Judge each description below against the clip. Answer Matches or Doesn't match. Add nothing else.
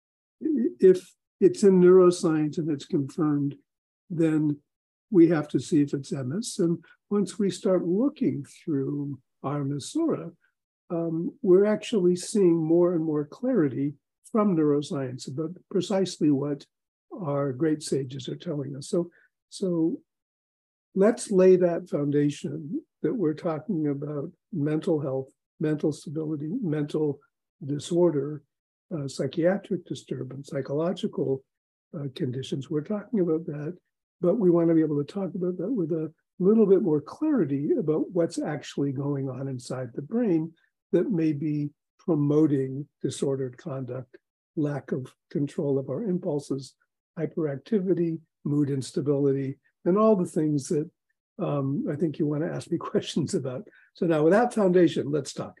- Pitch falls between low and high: Matches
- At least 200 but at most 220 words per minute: Doesn't match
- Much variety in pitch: Doesn't match